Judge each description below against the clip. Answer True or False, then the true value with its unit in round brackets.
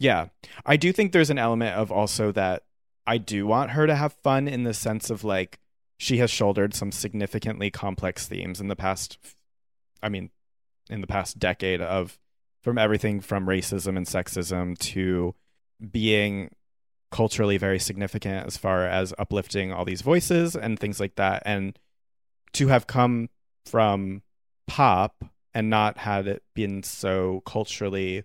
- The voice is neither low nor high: False (100 Hz)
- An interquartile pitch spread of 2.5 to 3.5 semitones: True (2.8 semitones)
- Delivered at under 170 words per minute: True (155 wpm)